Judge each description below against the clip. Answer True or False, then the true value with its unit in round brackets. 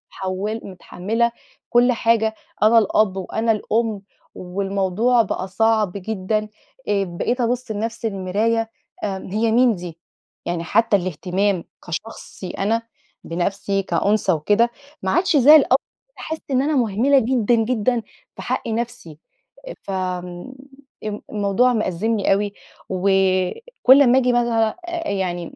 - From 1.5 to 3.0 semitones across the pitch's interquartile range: False (3.6 semitones)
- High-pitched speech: True (215 Hz)